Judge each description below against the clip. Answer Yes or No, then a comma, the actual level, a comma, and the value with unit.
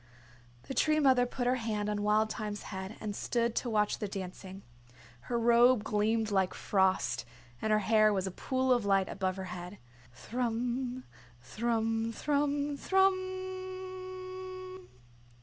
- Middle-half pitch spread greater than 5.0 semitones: Yes, wide, 5.4 semitones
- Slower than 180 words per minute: Yes, average, 140 wpm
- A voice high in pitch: Yes, high, 230 Hz